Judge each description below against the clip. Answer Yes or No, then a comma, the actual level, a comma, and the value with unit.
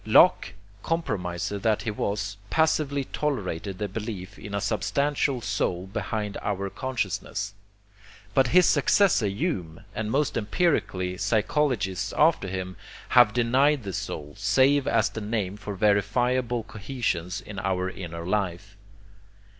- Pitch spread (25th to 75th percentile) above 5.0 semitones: Yes, wide, 5.4 semitones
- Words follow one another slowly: Yes, slow, 125 wpm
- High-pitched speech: No, low, 105 Hz